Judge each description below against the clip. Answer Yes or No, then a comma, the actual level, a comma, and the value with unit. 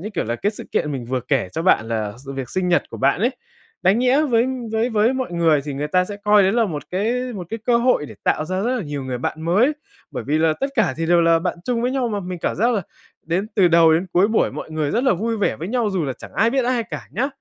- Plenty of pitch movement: Yes, wide, 6.7 semitones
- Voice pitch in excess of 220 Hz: No, medium, 185 Hz